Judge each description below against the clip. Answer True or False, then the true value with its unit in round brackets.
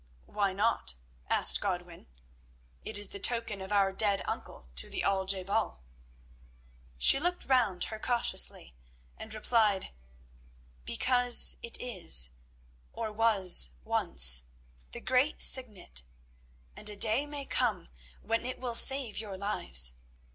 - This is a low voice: False (210 Hz)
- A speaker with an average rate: False (130 wpm)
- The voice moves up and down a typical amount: True (4.1 semitones)